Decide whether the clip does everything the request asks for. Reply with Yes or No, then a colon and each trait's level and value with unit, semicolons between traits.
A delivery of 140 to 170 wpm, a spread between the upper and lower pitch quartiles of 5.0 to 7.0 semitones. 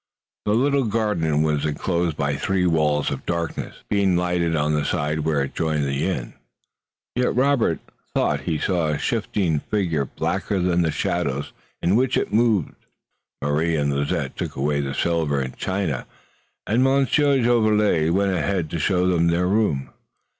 Yes: average, 165 wpm; average, 5.3 semitones